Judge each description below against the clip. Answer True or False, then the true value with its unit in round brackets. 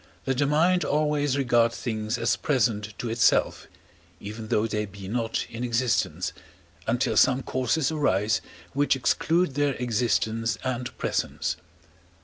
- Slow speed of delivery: True (130 wpm)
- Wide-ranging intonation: False (4.0 semitones)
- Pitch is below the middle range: True (120 Hz)